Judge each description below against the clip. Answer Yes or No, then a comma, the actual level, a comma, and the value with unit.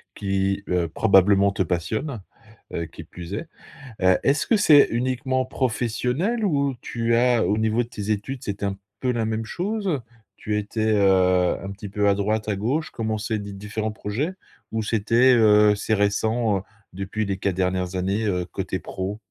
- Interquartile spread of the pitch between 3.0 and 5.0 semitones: Yes, average, 3.6 semitones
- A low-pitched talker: Yes, low, 105 Hz